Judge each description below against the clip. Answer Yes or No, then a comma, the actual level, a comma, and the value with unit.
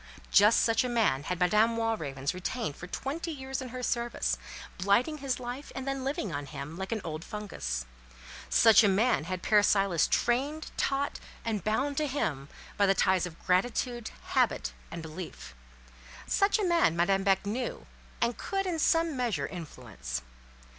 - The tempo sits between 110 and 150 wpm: No, average, 165 wpm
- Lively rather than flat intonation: Yes, wide, 6.9 semitones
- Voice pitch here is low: No, high, 215 Hz